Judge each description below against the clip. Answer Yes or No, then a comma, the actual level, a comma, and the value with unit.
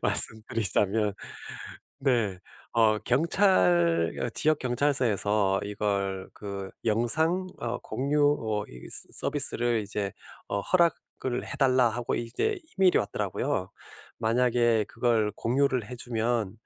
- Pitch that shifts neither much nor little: Yes, average, 3.9 semitones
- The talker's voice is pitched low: Yes, low, 115 Hz